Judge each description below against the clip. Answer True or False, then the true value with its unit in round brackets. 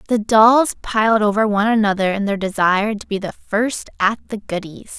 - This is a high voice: True (210 Hz)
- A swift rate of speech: False (195 wpm)